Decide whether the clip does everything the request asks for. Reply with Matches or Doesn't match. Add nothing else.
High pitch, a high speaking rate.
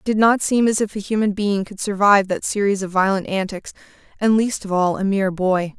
Matches